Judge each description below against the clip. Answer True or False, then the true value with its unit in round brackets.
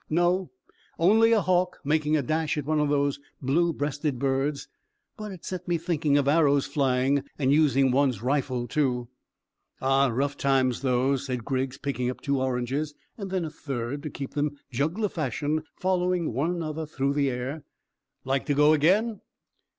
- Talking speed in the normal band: True (170 wpm)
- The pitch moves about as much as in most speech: True (3.1 semitones)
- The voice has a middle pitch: True (145 Hz)